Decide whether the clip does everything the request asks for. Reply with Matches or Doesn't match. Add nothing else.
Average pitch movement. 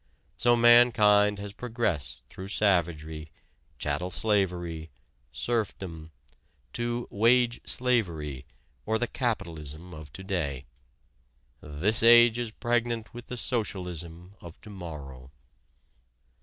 Doesn't match